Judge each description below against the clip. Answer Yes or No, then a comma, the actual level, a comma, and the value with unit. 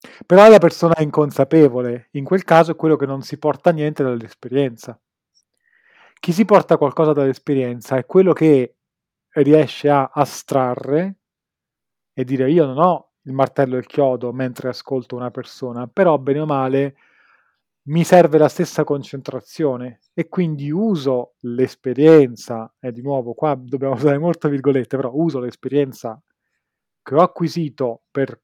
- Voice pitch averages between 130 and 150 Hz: Yes, medium, 140 Hz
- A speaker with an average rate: Yes, average, 150 wpm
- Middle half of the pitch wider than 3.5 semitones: Yes, average, 4.0 semitones